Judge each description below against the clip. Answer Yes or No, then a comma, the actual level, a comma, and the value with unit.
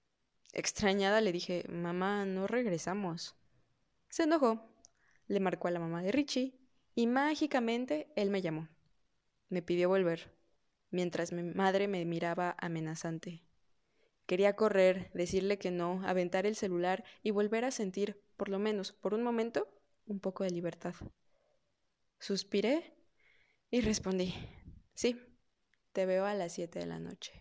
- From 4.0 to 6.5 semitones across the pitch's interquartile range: No, average, 3.6 semitones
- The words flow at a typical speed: Yes, average, 140 wpm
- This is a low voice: No, high, 190 Hz